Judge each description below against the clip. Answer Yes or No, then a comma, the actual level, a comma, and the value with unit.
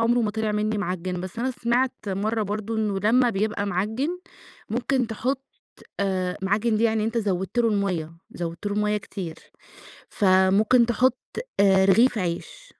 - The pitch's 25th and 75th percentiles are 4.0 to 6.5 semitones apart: No, average, 3.3 semitones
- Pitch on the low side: No, high, 210 Hz